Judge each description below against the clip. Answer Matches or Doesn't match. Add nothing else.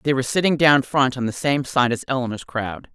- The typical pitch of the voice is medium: Doesn't match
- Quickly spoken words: Matches